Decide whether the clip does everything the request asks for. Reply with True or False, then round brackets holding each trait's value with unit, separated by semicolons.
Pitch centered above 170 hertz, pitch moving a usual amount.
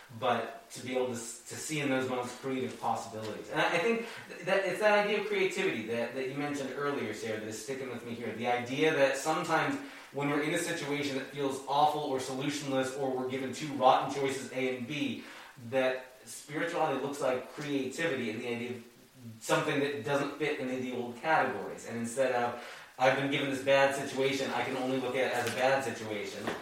False (135 Hz; 3.0 semitones)